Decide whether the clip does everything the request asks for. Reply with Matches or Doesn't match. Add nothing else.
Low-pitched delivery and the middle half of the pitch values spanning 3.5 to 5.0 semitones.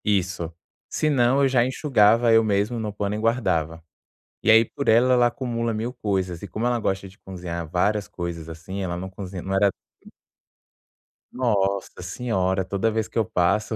Matches